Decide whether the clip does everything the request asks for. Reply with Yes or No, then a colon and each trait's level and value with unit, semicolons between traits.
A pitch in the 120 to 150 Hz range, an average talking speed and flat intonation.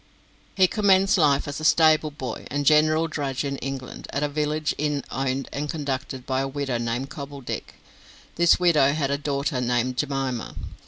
Yes: medium, 140 Hz; average, 170 wpm; narrow, 2.3 semitones